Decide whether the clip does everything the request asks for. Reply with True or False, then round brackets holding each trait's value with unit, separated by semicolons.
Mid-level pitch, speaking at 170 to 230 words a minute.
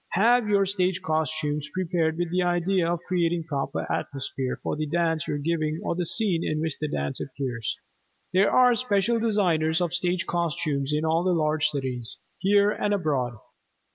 True (165 Hz; 175 wpm)